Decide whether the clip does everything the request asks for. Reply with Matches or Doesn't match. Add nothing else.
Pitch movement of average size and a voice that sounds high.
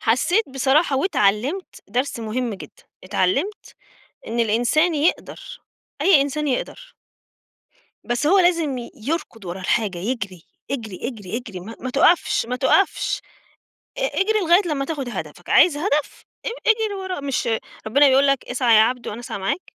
Doesn't match